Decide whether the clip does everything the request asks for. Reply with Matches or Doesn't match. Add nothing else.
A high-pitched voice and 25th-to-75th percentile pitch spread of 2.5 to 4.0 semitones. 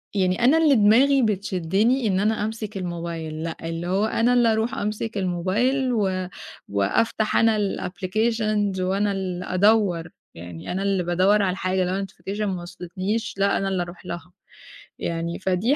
Matches